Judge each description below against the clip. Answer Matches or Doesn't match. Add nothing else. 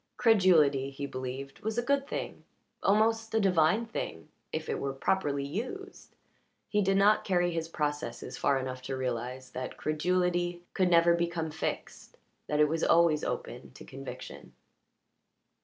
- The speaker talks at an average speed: Matches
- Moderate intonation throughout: Doesn't match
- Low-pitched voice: Doesn't match